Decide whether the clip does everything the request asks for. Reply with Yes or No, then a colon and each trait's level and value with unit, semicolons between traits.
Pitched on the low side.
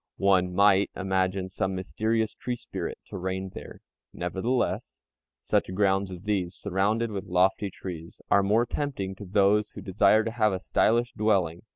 Yes: low, 100 Hz